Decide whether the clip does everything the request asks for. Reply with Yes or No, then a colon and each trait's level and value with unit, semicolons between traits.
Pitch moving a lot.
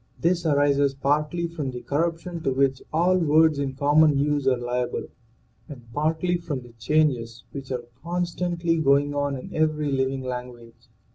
No: average, 3.5 semitones